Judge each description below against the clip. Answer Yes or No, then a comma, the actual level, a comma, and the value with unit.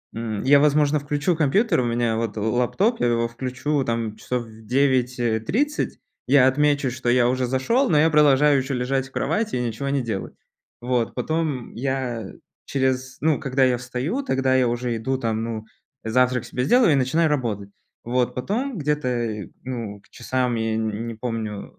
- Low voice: Yes, low, 125 Hz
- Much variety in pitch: No, average, 3.5 semitones